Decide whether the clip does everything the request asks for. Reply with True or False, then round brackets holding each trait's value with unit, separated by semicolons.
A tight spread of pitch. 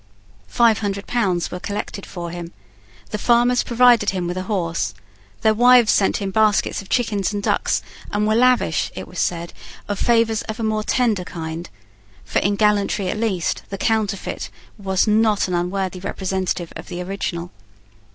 False (3.3 semitones)